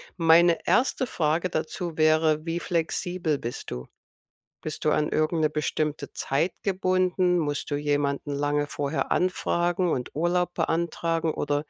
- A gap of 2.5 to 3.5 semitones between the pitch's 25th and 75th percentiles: Yes, average, 2.9 semitones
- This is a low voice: No, medium, 160 Hz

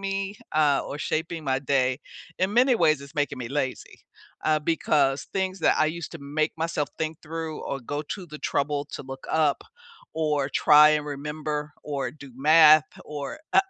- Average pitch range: No, narrow, 2.2 semitones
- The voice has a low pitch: No, medium, 150 Hz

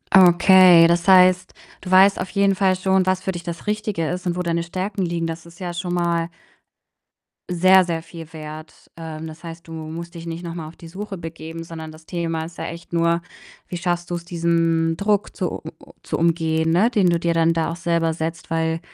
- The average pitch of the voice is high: No, medium, 170 Hz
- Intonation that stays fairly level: Yes, narrow, 1.8 semitones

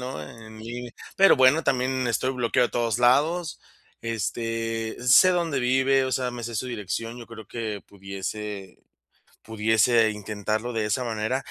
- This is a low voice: Yes, low, 115 Hz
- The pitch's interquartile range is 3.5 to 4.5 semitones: No, average, 2.7 semitones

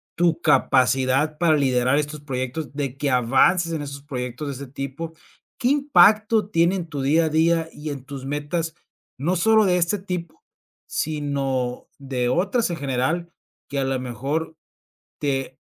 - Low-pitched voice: No, medium, 150 Hz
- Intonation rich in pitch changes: No, average, 4.0 semitones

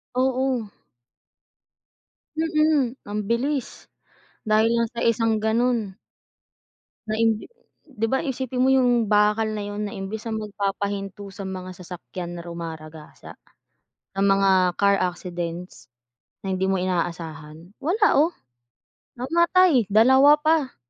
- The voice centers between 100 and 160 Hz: No, high, 215 Hz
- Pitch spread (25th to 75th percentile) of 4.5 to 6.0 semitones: Yes, average, 5.3 semitones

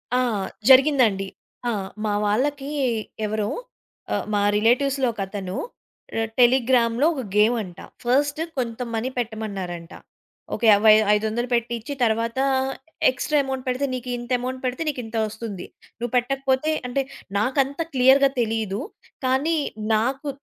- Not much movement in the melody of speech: No, average, 3.4 semitones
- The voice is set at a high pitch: Yes, high, 240 Hz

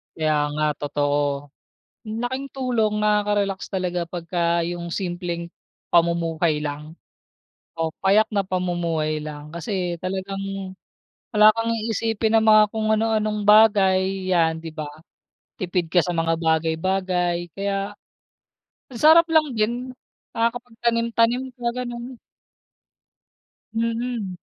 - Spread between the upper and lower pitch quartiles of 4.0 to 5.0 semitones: Yes, average, 4.7 semitones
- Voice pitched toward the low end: No, high, 190 Hz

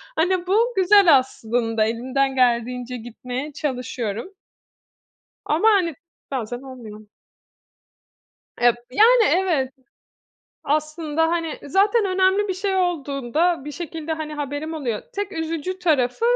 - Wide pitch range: Yes, wide, 6.5 semitones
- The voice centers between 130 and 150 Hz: No, very high, 305 Hz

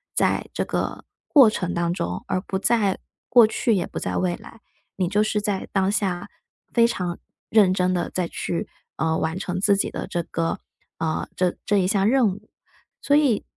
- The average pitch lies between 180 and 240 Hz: Yes, high, 190 Hz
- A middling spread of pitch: Yes, average, 3.3 semitones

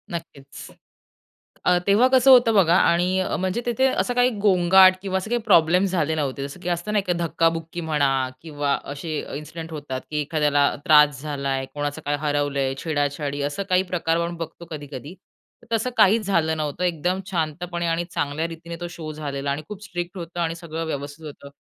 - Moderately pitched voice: Yes, medium, 165 Hz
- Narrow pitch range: No, average, 3.8 semitones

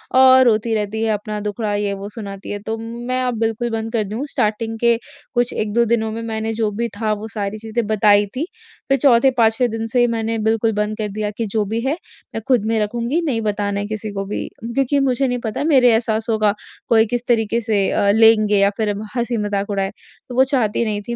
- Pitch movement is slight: Yes, narrow, 2.1 semitones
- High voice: Yes, high, 225 Hz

